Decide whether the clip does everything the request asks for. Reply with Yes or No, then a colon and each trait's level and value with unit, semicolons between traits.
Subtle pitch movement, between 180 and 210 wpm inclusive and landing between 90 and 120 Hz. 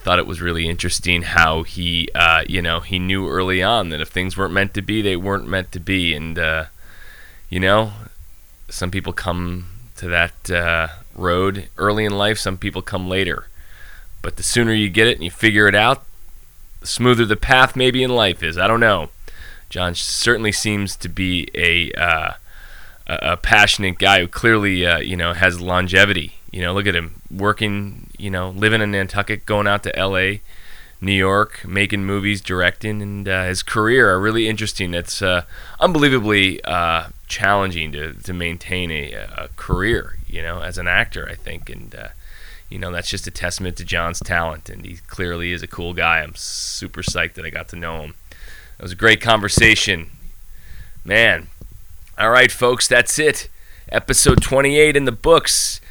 No: average, 3.2 semitones; average, 185 wpm; very low, 95 Hz